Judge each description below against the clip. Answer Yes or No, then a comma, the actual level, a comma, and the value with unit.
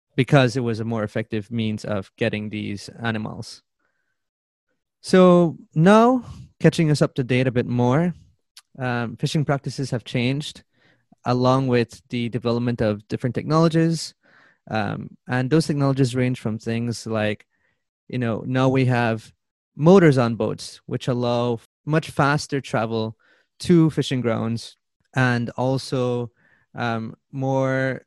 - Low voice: Yes, low, 125 Hz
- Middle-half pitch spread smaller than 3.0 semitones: No, average, 3.6 semitones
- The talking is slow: Yes, slow, 130 wpm